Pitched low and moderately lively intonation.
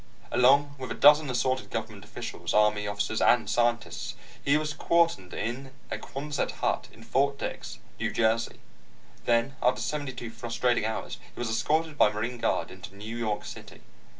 Yes: low, 120 Hz; average, 3.9 semitones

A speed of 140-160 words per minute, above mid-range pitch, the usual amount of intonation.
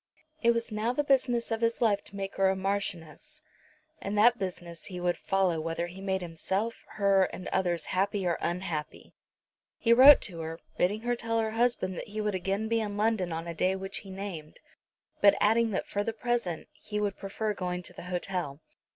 No: fast, 205 wpm; high, 195 Hz; average, 3.7 semitones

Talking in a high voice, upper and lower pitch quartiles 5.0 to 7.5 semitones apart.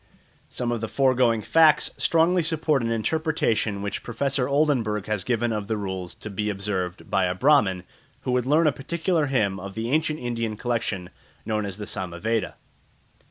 No: low, 115 Hz; wide, 5.6 semitones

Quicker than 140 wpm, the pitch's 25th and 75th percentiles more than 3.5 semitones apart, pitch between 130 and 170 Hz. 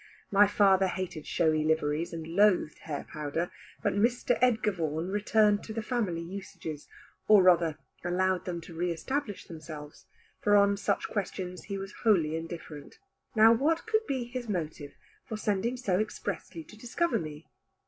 No: average, 160 wpm; average, 4.7 semitones; high, 190 Hz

